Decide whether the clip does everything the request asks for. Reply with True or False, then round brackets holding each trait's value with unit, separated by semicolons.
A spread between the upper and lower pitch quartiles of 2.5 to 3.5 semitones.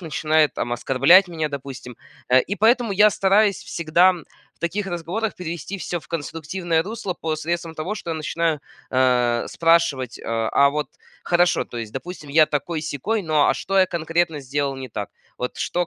False (4.1 semitones)